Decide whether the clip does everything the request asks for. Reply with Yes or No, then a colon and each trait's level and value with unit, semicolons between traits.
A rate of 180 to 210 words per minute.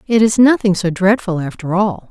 Yes: average, 200 wpm